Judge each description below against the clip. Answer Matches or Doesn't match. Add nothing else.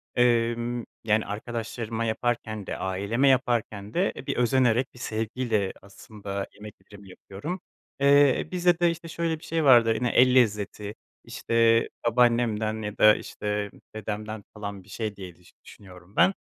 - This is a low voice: Matches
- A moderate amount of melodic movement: Matches